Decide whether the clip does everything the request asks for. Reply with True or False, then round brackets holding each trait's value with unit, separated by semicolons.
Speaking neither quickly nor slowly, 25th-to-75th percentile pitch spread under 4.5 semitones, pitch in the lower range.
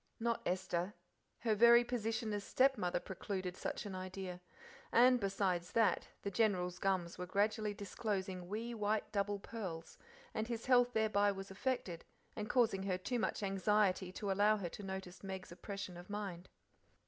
False (160 wpm; 2.8 semitones; 200 Hz)